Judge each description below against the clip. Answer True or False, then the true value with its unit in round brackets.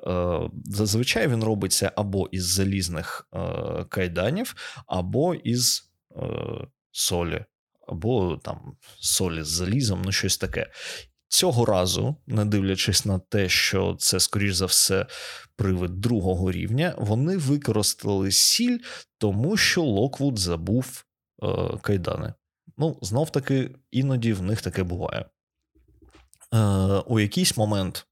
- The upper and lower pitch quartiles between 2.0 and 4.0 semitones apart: False (4.9 semitones)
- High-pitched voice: False (105 Hz)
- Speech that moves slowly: False (115 wpm)